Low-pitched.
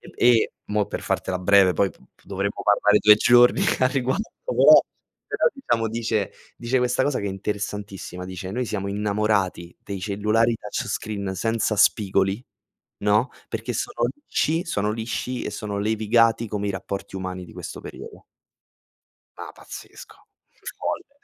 Yes: low, 105 Hz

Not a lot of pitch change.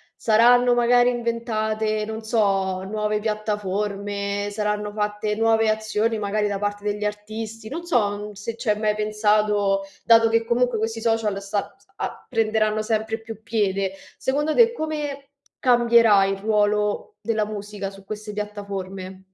Yes: narrow, 1.7 semitones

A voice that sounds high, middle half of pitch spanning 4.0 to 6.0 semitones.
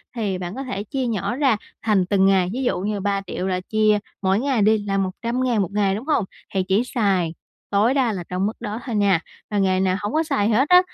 No: high, 205 Hz; average, 3.6 semitones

